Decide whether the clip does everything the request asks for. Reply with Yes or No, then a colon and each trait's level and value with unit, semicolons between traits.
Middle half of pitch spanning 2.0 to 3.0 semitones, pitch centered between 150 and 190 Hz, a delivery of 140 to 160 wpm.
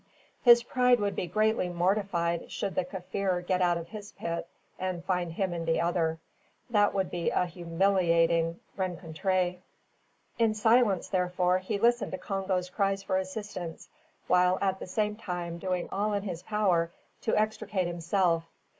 Yes: average, 2.7 semitones; medium, 185 Hz; average, 155 wpm